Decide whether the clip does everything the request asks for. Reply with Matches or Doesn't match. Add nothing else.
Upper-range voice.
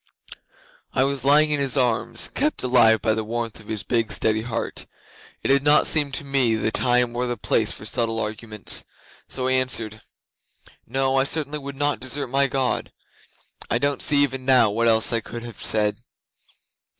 Doesn't match